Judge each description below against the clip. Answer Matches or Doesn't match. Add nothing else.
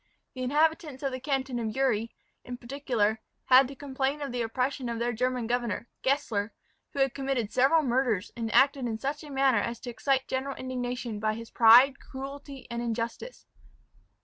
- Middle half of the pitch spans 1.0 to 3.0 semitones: Matches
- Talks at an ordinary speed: Matches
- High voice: Matches